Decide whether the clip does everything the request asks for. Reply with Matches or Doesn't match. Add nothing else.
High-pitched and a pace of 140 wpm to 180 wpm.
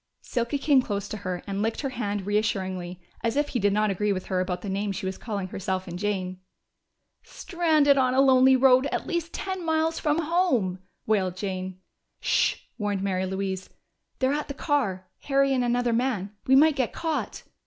Doesn't match